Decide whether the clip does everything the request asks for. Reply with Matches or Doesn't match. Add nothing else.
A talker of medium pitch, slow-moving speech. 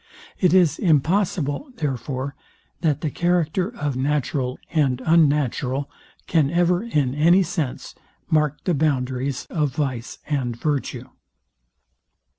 Matches